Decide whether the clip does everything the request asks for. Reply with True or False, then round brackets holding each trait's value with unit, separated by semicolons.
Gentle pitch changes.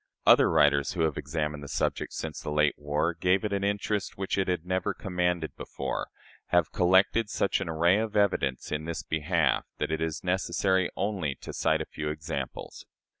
False (3.9 semitones)